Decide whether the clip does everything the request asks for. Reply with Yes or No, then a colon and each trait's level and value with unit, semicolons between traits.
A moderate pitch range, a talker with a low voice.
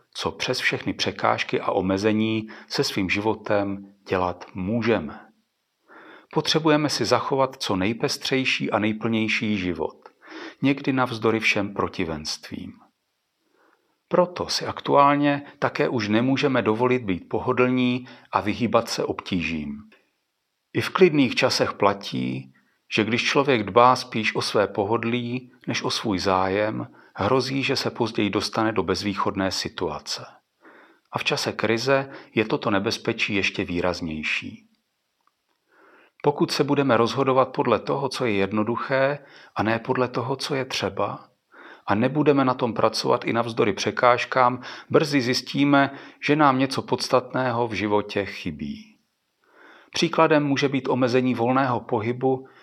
Yes: average, 4.5 semitones; low, 125 Hz